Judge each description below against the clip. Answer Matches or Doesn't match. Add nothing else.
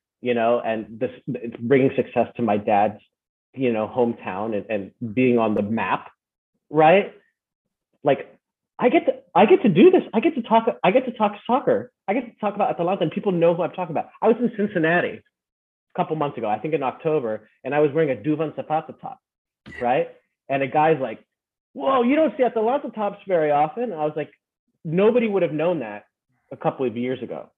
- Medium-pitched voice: Matches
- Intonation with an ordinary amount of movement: Doesn't match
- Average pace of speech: Doesn't match